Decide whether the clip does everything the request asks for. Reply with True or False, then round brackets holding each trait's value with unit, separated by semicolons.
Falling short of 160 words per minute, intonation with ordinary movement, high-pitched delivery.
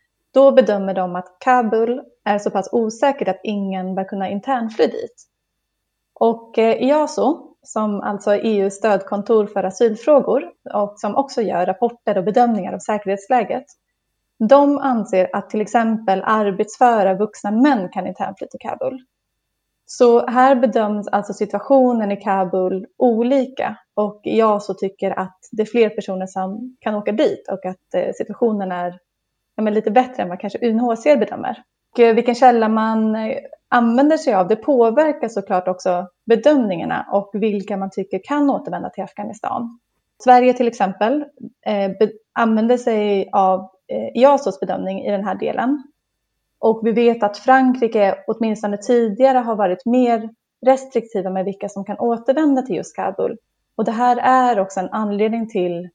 True (145 wpm; 4.1 semitones; 220 Hz)